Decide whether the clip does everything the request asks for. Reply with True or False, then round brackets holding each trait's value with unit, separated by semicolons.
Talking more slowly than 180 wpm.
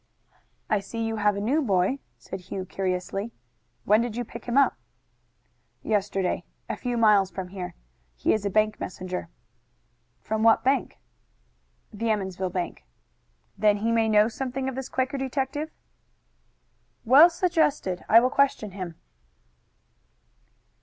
True (140 wpm)